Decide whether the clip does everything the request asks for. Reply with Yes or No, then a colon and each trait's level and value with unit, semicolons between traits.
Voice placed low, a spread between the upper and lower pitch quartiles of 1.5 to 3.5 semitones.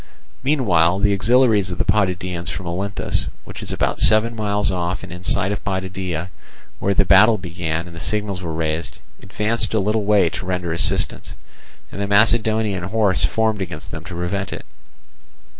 Yes: very low, 95 Hz; average, 3.2 semitones